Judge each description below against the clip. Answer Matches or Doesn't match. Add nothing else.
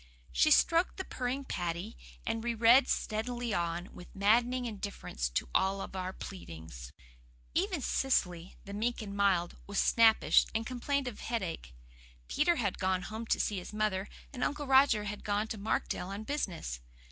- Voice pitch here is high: Matches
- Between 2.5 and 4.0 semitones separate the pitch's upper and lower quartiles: Doesn't match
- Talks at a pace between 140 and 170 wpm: Matches